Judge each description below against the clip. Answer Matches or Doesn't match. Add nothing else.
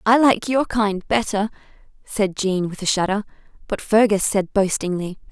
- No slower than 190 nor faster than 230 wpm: Doesn't match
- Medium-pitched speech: Doesn't match